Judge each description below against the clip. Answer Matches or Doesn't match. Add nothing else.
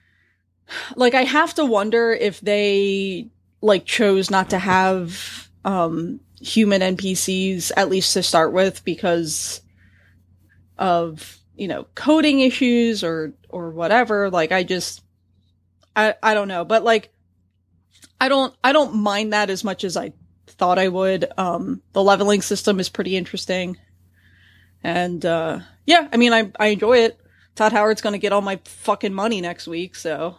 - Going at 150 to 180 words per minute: Matches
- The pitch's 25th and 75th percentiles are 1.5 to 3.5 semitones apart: Doesn't match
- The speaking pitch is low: Doesn't match